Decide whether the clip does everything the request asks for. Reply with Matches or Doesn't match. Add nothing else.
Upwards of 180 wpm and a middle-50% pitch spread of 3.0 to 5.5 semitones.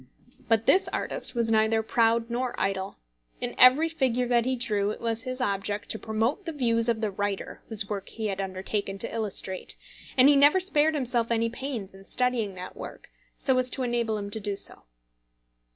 Matches